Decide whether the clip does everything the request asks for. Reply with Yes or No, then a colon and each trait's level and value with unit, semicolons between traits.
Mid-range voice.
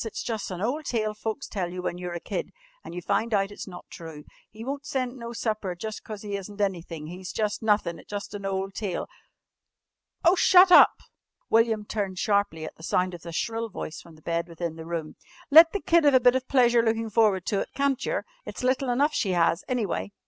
No: high, 210 Hz